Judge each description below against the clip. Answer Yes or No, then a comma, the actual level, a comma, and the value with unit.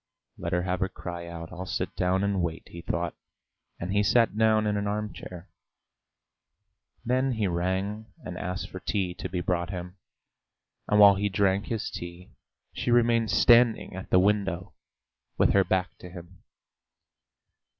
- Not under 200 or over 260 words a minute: No, average, 165 wpm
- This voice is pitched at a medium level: No, very low, 95 Hz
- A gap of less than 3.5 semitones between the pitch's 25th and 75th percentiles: Yes, average, 2.8 semitones